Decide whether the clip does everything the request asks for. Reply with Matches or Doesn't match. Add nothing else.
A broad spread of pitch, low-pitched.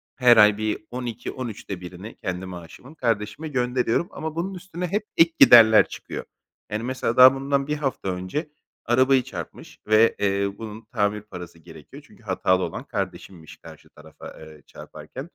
Matches